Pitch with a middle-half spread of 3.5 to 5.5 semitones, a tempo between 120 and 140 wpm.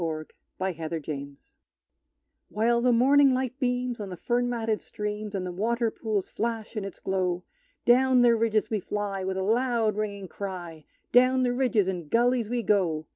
No: average, 4.4 semitones; average, 180 wpm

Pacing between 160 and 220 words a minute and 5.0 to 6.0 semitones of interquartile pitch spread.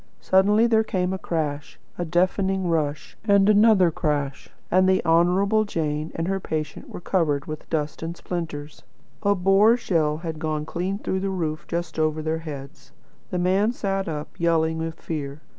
No: average, 170 wpm; average, 3.6 semitones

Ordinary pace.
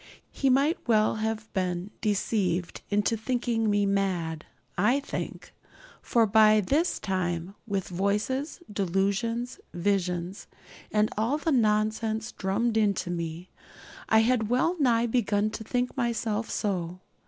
No: slow, 125 wpm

